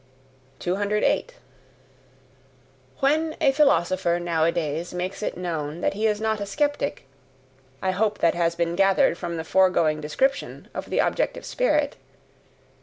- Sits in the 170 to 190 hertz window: Yes, medium, 185 Hz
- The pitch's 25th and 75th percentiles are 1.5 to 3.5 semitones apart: No, average, 3.9 semitones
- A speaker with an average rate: No, slow, 125 wpm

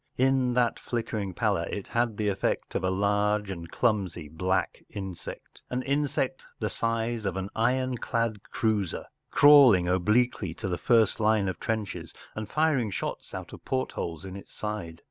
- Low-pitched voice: Yes, low, 105 Hz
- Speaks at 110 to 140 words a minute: No, average, 160 wpm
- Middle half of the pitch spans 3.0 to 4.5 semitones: Yes, average, 4.1 semitones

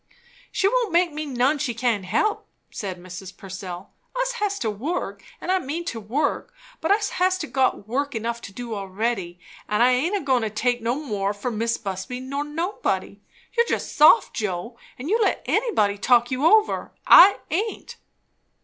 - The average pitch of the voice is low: No, very high, 250 Hz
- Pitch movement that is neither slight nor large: No, wide, 8.3 semitones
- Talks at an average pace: Yes, average, 180 wpm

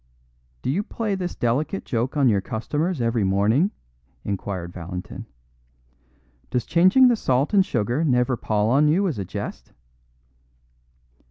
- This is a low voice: Yes, low, 125 Hz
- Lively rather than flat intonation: Yes, wide, 8.1 semitones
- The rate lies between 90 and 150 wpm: Yes, average, 140 wpm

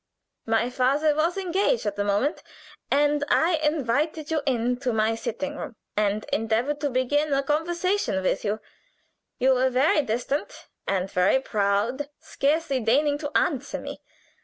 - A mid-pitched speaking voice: No, very high, 270 Hz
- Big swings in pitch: No, average, 4.9 semitones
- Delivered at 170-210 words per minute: No, average, 145 wpm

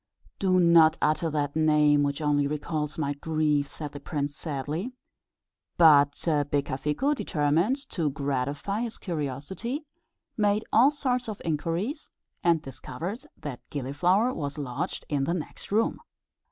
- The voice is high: No, medium, 155 Hz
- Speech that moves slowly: Yes, slow, 130 wpm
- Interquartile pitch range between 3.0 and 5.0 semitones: Yes, average, 4.6 semitones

